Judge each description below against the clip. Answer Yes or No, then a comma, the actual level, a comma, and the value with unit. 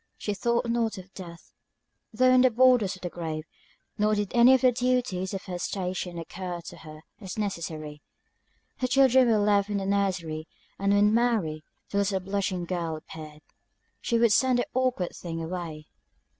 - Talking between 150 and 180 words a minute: Yes, average, 175 wpm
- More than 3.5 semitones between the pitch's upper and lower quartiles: Yes, average, 5.3 semitones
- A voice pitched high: Yes, high, 195 Hz